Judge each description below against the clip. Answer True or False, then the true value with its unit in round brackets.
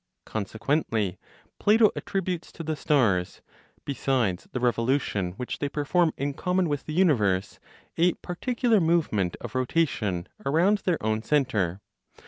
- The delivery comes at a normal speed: False (125 wpm)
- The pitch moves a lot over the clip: True (7.8 semitones)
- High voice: False (140 Hz)